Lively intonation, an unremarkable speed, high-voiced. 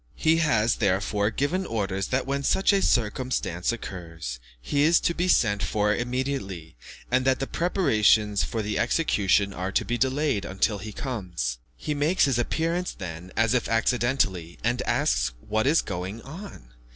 No: wide, 6.0 semitones; average, 165 wpm; low, 115 Hz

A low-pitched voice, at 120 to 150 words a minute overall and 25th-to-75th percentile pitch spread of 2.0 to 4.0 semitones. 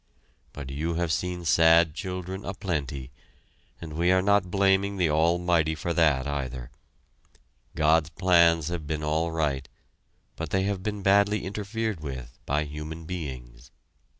Yes: very low, 80 Hz; average, 145 wpm; average, 3.6 semitones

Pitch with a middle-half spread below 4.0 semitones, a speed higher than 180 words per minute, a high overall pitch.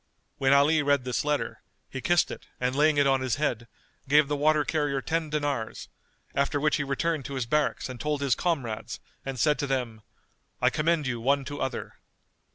No: narrow, 2.4 semitones; average, 195 wpm; medium, 140 Hz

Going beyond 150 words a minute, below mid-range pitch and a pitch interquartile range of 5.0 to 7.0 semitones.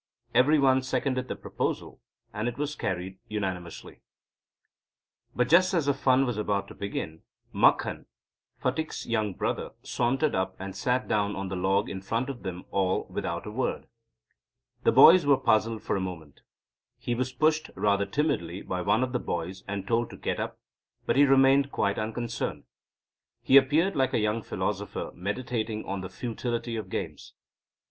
Yes: average, 170 wpm; low, 115 Hz; average, 5.3 semitones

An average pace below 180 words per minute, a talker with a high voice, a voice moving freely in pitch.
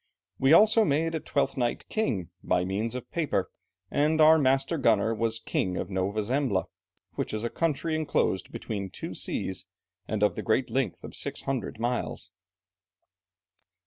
No: average, 160 wpm; low, 125 Hz; wide, 6.3 semitones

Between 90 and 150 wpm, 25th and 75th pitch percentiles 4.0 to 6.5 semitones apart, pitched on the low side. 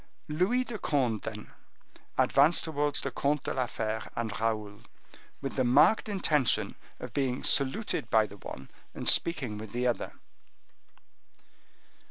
Yes: average, 145 wpm; average, 5.3 semitones; low, 130 Hz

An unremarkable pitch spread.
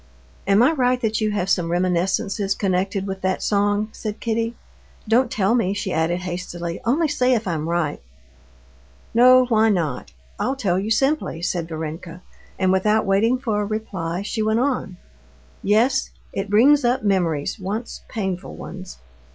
Yes: average, 3.9 semitones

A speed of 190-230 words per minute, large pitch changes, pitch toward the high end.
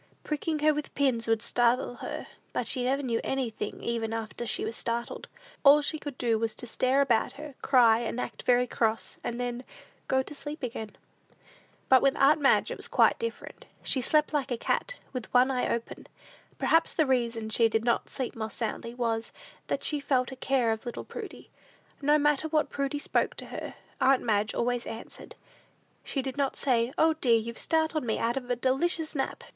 No: average, 195 wpm; average, 3.4 semitones; very high, 250 Hz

